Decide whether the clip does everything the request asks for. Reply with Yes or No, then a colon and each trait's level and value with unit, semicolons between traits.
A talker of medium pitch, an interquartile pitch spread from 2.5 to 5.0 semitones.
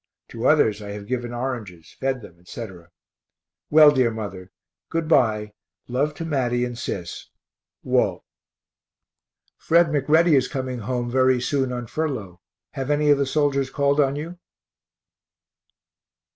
No: low, 130 Hz; average, 4.5 semitones